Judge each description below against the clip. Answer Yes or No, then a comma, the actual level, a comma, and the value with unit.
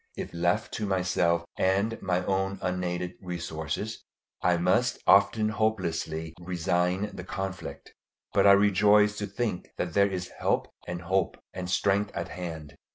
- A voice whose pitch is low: Yes, very low, 95 Hz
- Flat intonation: Yes, narrow, 2.3 semitones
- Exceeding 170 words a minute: No, average, 145 wpm